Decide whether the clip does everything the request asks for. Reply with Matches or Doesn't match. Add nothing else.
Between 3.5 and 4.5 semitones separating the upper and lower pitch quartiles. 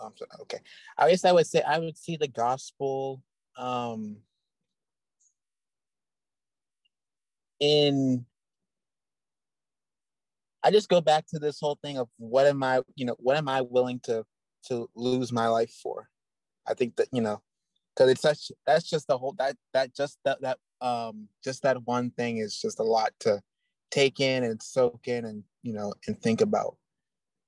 Matches